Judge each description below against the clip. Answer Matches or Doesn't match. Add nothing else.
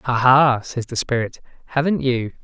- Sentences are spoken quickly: Doesn't match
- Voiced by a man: Matches